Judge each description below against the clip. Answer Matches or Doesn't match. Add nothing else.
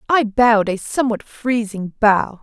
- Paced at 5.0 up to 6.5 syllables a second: Doesn't match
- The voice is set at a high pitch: Matches